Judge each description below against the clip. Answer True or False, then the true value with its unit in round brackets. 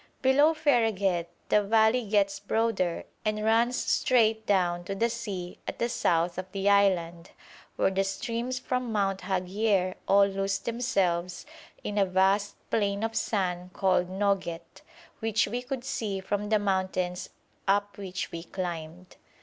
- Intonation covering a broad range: False (3.3 semitones)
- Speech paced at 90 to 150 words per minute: True (145 wpm)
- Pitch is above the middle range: True (200 Hz)